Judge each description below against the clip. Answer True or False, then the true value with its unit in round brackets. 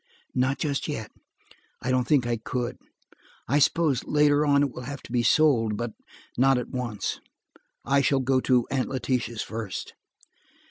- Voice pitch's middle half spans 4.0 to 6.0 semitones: False (2.9 semitones)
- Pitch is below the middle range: True (130 Hz)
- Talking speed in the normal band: True (155 wpm)